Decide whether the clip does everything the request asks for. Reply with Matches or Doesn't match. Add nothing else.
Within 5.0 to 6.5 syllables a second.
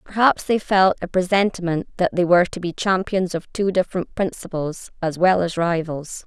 Matches